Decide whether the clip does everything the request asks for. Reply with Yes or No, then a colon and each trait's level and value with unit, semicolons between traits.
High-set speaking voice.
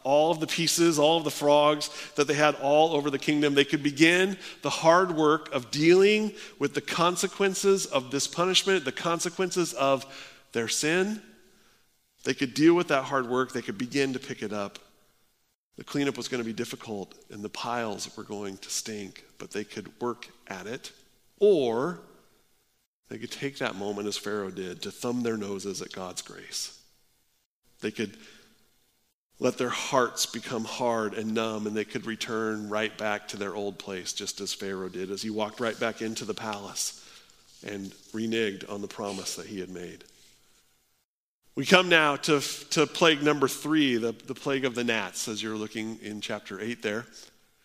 No: low, 130 Hz